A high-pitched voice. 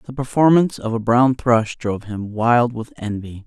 No: low, 120 Hz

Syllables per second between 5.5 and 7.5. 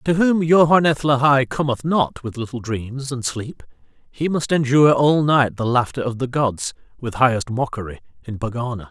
No: 5.0 syllables/s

